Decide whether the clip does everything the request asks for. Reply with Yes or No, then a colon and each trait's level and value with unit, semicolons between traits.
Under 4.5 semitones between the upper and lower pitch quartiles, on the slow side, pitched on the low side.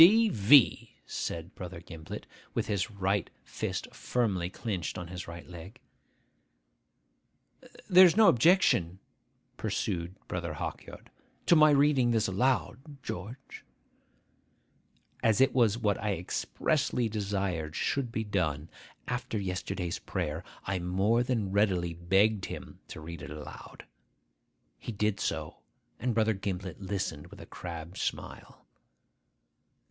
No: average, 5.0 semitones; slow, 120 wpm; low, 100 Hz